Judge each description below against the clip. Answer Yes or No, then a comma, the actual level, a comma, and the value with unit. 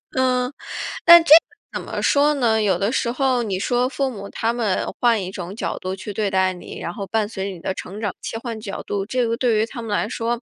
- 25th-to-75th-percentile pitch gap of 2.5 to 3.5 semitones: No, average, 4.0 semitones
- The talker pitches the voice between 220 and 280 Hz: Yes, high, 225 Hz